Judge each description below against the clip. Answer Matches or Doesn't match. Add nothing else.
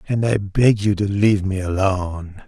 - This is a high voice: Doesn't match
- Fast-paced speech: Doesn't match